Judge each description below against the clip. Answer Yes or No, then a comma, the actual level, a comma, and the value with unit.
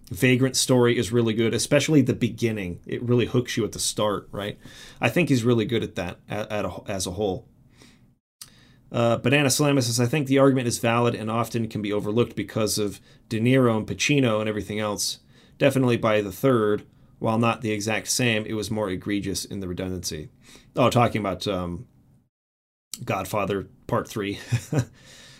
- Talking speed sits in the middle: Yes, average, 175 wpm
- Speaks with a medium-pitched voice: No, low, 115 Hz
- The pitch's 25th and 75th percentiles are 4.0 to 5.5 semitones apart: No, average, 3.2 semitones